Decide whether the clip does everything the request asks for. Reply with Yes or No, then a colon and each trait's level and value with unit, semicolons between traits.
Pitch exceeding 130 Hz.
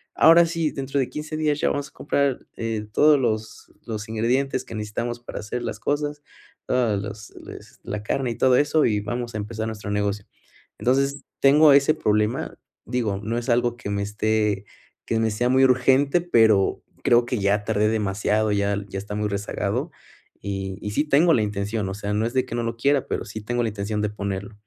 No: low, 115 Hz